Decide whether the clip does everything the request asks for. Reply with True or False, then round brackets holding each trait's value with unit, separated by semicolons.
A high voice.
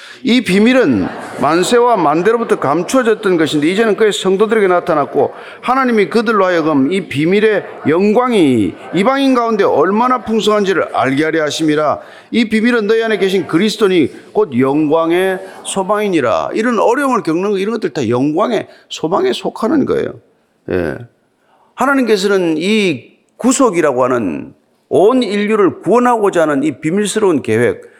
True (215 Hz)